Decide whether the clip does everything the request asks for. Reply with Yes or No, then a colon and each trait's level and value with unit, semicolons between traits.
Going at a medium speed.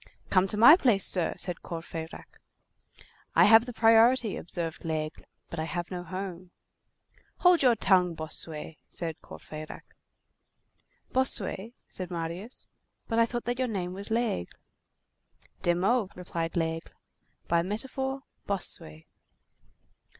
No: slow, 125 wpm